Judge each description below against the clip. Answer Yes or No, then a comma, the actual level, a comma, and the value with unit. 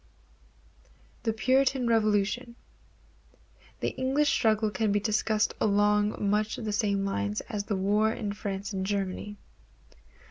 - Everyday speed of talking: No, slow, 120 wpm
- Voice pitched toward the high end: Yes, high, 210 Hz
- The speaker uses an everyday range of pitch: No, narrow, 1.6 semitones